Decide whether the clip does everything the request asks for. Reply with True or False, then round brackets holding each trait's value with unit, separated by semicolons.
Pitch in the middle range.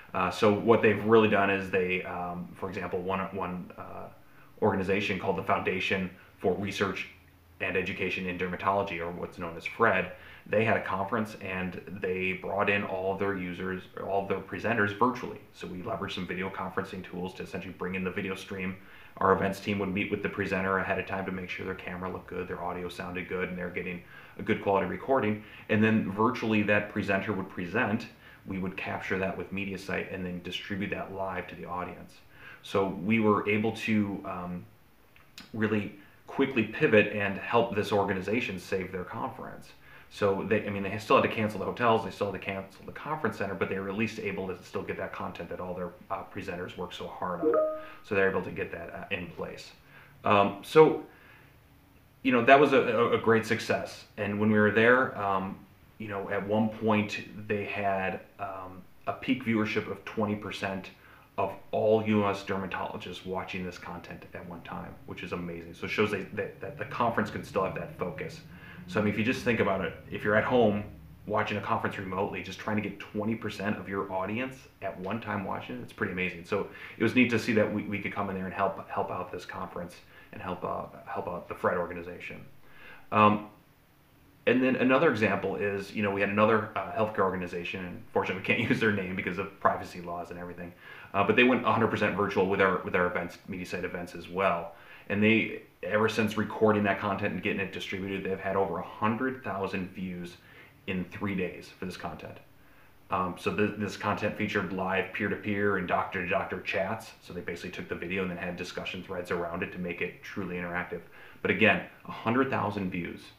False (100 Hz)